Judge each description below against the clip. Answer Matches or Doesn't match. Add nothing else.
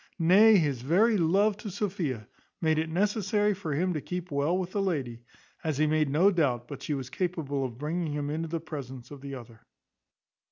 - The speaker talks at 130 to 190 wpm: Doesn't match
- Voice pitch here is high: Doesn't match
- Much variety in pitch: Doesn't match